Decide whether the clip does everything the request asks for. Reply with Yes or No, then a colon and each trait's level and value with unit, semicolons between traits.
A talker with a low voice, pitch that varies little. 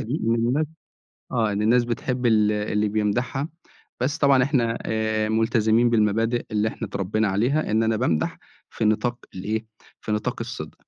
Yes: low, 110 Hz; narrow, 2.3 semitones